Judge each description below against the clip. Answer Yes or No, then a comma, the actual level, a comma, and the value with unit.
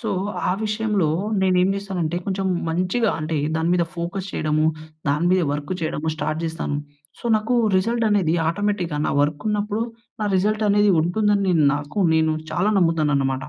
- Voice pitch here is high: No, medium, 180 Hz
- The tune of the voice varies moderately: Yes, average, 4.5 semitones